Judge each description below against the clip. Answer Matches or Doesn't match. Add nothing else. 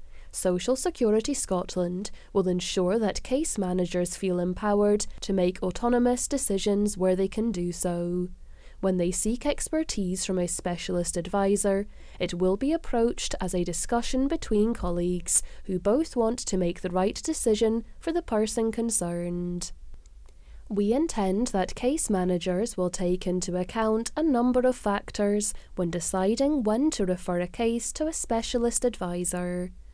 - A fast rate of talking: Doesn't match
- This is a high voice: Matches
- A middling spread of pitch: Matches